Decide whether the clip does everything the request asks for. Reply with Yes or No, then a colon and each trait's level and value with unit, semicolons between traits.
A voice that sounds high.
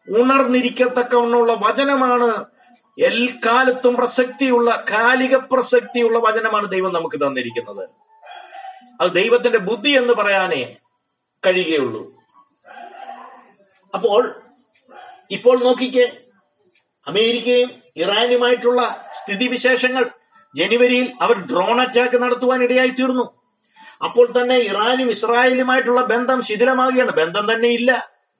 Yes: very high, 250 Hz